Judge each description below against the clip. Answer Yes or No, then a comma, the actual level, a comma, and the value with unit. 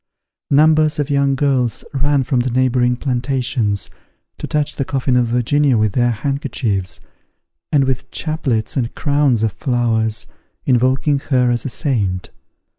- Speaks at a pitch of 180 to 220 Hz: No, low, 130 Hz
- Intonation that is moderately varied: Yes, average, 3.0 semitones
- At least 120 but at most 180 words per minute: Yes, average, 140 wpm